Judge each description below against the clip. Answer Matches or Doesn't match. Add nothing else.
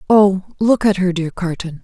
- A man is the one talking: Doesn't match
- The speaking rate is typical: Matches